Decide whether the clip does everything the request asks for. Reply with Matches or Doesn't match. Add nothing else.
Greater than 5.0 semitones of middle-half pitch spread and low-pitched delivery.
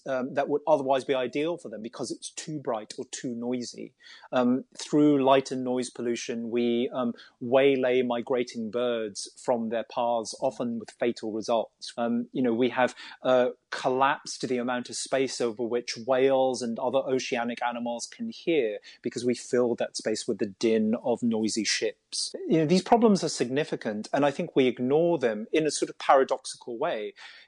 Doesn't match